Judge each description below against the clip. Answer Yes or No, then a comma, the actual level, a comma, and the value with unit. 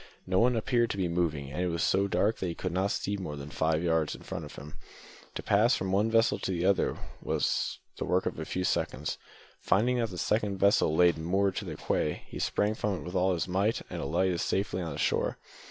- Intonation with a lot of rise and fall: No, average, 3.0 semitones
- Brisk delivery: Yes, fast, 240 wpm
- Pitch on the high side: No, very low, 95 Hz